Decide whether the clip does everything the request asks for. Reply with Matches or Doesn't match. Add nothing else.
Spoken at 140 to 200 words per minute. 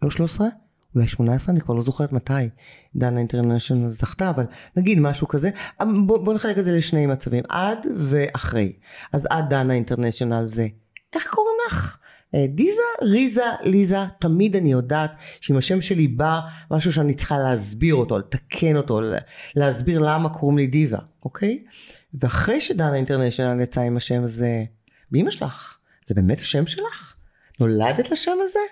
Matches